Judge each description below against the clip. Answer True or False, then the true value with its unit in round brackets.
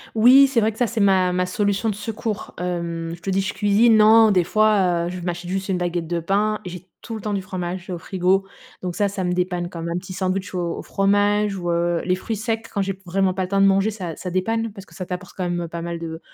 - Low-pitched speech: False (190 Hz)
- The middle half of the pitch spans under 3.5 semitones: True (2.8 semitones)